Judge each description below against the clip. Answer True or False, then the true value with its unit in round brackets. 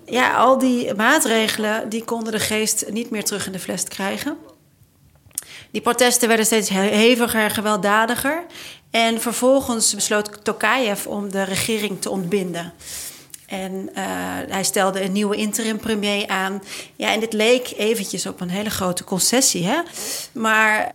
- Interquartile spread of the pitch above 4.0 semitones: False (2.9 semitones)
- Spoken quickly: False (150 wpm)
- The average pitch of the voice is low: False (215 Hz)